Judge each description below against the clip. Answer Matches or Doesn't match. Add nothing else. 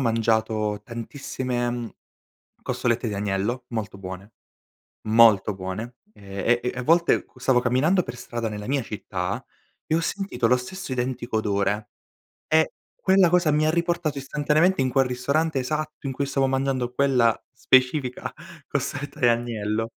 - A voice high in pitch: Doesn't match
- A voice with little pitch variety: Doesn't match